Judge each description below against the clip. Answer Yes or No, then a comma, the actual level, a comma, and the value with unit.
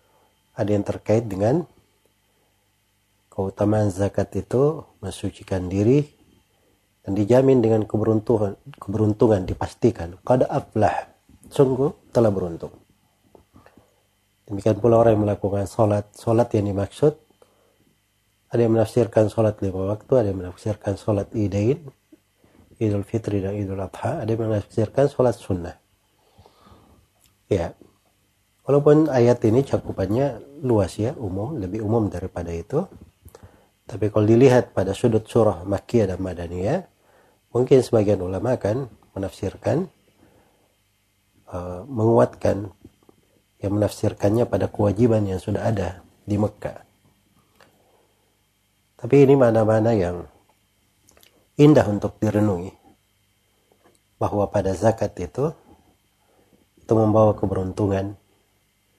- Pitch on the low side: Yes, low, 105 Hz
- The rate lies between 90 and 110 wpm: Yes, average, 105 wpm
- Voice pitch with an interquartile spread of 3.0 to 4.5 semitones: No, narrow, 2.5 semitones